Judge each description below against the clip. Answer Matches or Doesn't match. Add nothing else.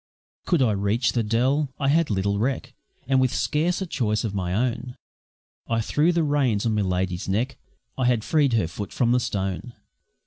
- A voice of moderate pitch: Doesn't match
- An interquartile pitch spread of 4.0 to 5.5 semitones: Matches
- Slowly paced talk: Doesn't match